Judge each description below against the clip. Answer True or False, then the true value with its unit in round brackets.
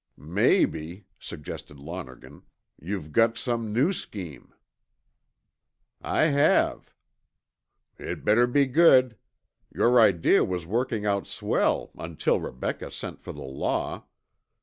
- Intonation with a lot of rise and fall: True (6.9 semitones)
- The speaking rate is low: True (105 wpm)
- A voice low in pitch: True (105 Hz)